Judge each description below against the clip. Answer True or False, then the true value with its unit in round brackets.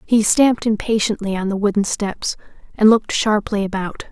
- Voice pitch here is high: True (210 Hz)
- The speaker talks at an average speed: True (160 wpm)